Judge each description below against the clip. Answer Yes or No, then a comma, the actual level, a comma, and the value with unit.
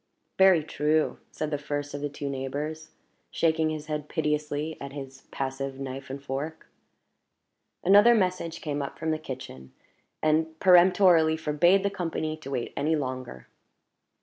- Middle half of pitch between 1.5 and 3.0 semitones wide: Yes, narrow, 2.6 semitones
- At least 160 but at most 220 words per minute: No, average, 150 wpm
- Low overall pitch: No, medium, 150 Hz